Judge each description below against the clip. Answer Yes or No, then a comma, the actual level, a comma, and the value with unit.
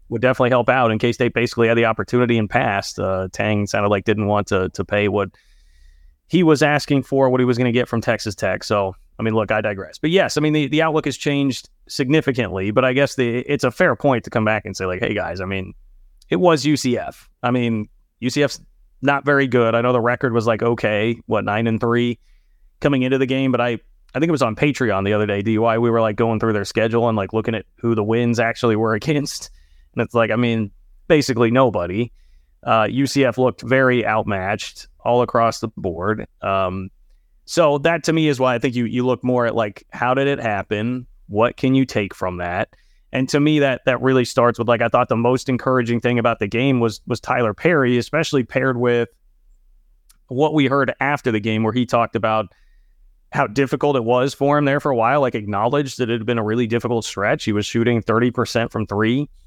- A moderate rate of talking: No, fast, 225 wpm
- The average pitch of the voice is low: Yes, low, 120 Hz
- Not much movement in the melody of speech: No, average, 3.4 semitones